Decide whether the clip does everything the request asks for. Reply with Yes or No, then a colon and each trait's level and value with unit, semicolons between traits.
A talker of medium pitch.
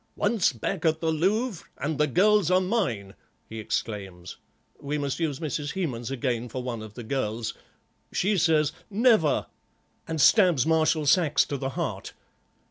Yes: medium, 150 Hz